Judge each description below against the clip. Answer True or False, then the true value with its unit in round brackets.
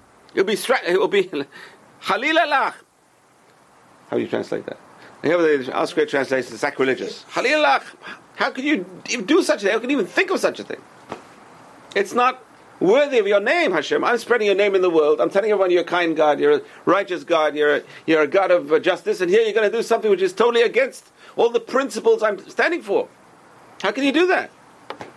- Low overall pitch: False (225 Hz)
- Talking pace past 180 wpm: True (205 wpm)